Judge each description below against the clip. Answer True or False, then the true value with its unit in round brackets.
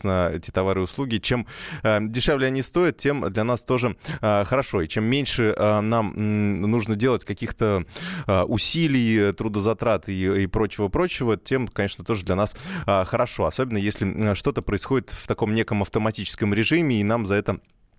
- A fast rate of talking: True (175 wpm)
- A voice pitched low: True (110 Hz)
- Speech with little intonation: False (3.6 semitones)